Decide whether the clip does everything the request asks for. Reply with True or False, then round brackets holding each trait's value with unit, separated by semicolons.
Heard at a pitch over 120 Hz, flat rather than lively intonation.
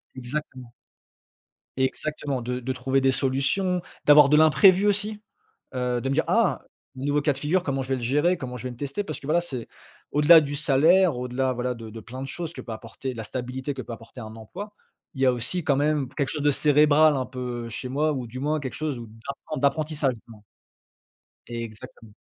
False (135 Hz; 3.4 semitones)